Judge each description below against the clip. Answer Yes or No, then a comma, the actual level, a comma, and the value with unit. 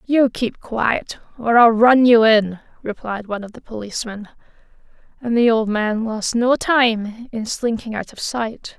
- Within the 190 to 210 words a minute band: No, average, 170 wpm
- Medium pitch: No, high, 225 Hz